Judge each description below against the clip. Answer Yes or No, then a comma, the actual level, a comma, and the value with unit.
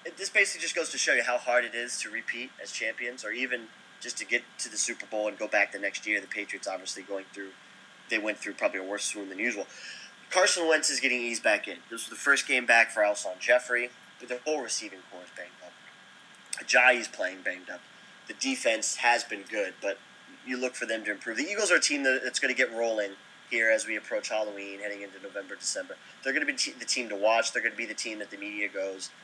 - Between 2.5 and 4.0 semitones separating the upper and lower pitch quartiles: Yes, average, 3.6 semitones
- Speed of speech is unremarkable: No, fast, 250 wpm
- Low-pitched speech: Yes, low, 115 Hz